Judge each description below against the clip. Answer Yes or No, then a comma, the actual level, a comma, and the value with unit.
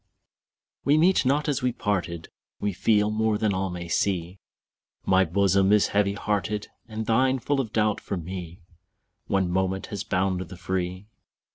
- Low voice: Yes, low, 100 Hz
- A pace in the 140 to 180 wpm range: Yes, average, 160 wpm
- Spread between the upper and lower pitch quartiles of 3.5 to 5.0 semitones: No, average, 2.8 semitones